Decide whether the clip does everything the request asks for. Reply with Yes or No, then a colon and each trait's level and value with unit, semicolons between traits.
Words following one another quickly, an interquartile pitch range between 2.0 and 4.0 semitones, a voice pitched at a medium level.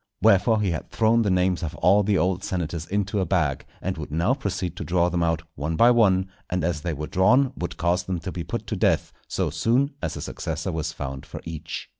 No: fast, 235 wpm; average, 3.4 semitones; very low, 90 Hz